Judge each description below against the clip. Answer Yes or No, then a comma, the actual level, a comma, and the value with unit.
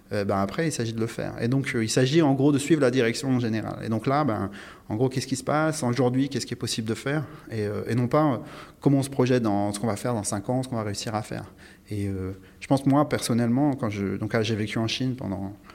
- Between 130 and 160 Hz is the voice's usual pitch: No, low, 120 Hz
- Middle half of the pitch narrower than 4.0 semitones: No, average, 4.4 semitones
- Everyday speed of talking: No, fast, 290 wpm